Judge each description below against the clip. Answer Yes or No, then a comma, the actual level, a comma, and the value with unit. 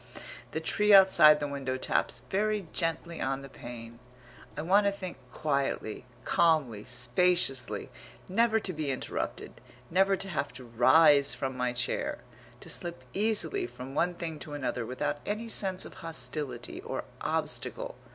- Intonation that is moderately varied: No, wide, 6.5 semitones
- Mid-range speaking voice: Yes, medium, 150 Hz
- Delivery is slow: No, average, 150 wpm